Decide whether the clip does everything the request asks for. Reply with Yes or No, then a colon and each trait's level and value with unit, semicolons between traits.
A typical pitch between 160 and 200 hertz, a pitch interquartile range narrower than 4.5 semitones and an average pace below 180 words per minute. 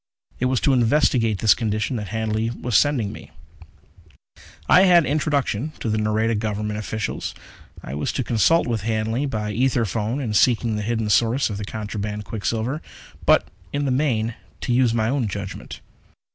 No: low, 115 Hz; average, 3.2 semitones; average, 170 wpm